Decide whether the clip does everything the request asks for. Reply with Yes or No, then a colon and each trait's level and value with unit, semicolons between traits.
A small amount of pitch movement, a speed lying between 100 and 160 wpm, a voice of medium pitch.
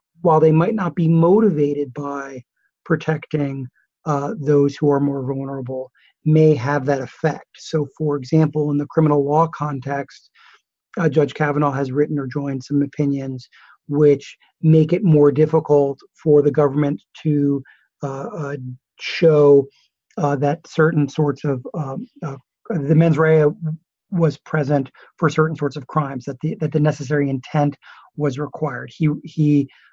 Yes: narrow, 1.9 semitones; average, 150 wpm; medium, 145 Hz